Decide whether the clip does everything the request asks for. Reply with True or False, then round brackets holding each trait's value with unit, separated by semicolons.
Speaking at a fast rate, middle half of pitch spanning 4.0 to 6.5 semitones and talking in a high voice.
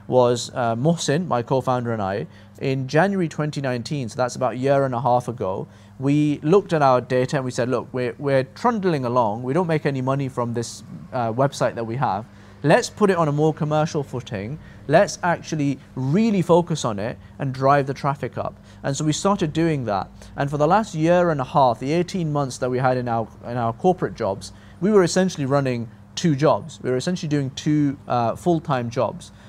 False (215 wpm; 4.6 semitones; 135 Hz)